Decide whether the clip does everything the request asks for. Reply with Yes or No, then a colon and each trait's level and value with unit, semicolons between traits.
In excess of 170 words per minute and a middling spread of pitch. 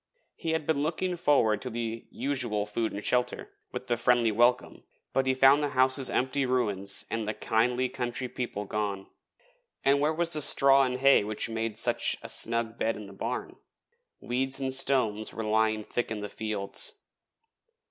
Yes: average, 180 wpm; average, 3.6 semitones